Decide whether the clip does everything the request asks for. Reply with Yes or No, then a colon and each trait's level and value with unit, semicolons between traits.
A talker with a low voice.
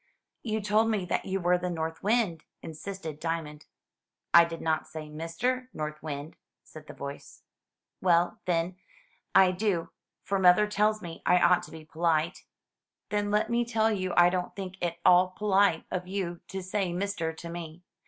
No: medium, 180 Hz